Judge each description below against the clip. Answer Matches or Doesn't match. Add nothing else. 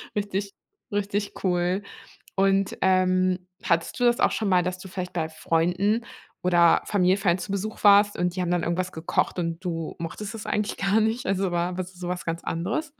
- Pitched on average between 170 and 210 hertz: Matches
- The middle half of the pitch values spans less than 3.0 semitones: Matches